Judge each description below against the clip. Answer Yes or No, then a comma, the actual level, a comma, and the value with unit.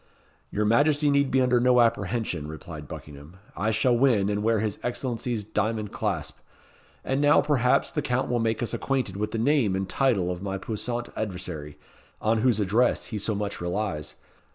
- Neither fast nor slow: Yes, average, 175 wpm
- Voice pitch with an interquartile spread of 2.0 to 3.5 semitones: No, average, 4.1 semitones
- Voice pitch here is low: Yes, low, 110 Hz